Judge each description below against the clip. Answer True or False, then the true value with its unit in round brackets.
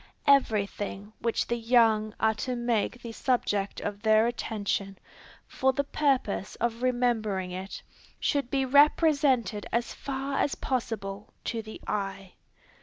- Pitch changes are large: False (3.7 semitones)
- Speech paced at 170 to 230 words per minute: False (135 wpm)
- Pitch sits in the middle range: False (230 Hz)